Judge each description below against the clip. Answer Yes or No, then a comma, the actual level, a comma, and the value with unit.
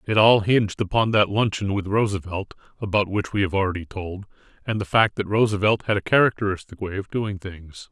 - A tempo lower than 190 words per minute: No, average, 195 wpm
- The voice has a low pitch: Yes, low, 100 Hz